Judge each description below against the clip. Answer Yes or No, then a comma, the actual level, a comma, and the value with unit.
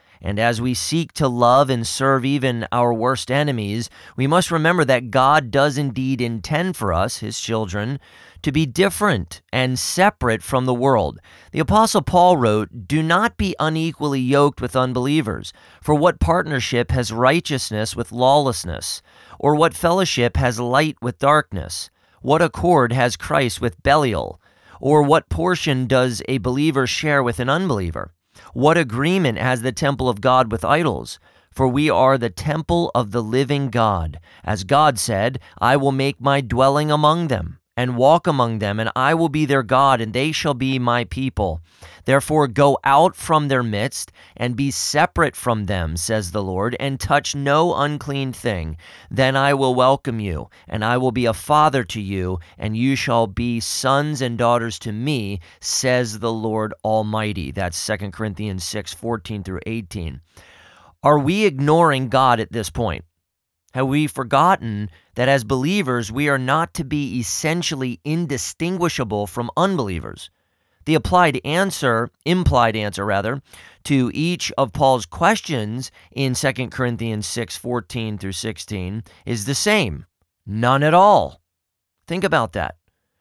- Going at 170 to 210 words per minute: No, average, 155 wpm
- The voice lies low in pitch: Yes, low, 125 Hz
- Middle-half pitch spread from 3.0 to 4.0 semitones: No, average, 5.0 semitones